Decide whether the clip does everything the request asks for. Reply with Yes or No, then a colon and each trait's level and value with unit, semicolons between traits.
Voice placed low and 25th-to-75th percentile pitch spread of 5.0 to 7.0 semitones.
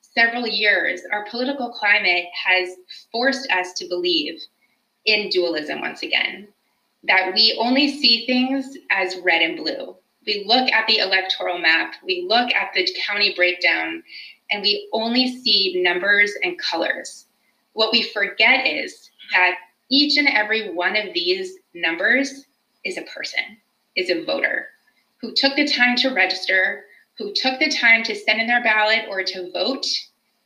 No: high, 220 Hz; average, 5.3 semitones